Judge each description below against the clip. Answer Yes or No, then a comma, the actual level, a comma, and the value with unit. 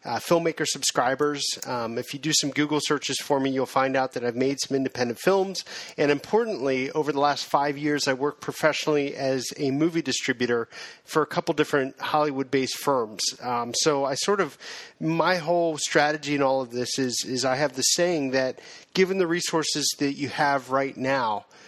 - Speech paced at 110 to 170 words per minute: No, average, 195 wpm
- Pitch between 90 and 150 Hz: Yes, medium, 140 Hz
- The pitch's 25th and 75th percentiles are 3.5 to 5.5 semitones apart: No, narrow, 2.6 semitones